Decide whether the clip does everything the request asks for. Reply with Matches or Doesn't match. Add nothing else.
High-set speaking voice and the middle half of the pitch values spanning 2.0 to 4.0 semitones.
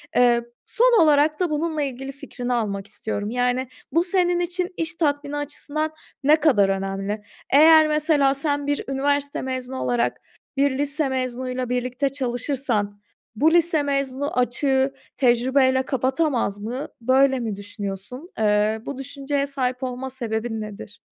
Matches